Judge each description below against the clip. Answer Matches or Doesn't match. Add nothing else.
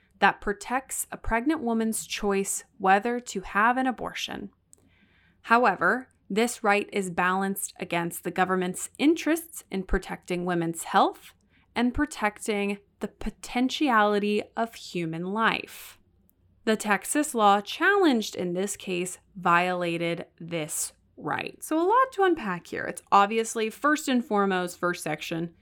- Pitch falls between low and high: Doesn't match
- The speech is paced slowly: Matches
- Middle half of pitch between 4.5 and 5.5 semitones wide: Matches